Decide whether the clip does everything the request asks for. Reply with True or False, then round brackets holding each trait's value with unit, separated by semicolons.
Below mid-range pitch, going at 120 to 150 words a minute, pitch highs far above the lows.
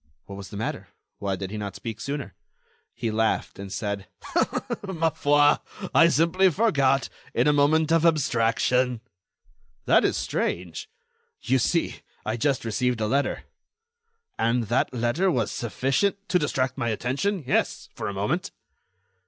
True (130 Hz; 145 wpm; 5.9 semitones)